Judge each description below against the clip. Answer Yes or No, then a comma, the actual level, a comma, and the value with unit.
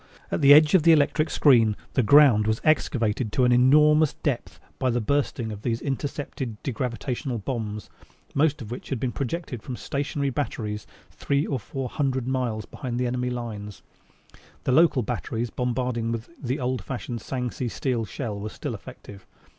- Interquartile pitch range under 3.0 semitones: No, average, 3.3 semitones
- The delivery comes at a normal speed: Yes, average, 170 wpm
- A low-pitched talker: Yes, low, 125 Hz